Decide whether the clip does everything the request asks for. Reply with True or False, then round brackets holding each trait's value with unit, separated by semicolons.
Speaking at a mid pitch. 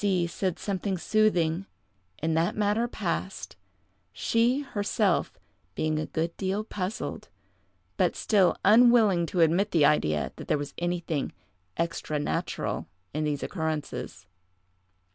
True (180 Hz)